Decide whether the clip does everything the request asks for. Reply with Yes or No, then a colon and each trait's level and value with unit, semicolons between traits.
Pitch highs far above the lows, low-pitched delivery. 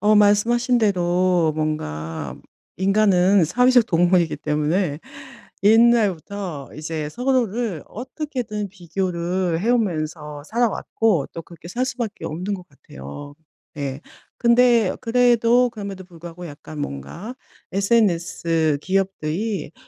No: wide, 6.1 semitones; medium, 185 Hz